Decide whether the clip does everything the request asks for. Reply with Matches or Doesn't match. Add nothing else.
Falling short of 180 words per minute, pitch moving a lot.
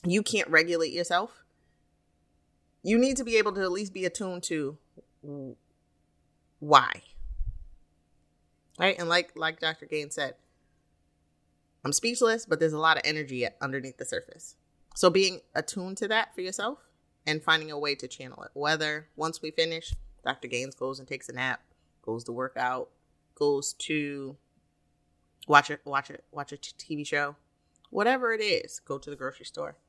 Matches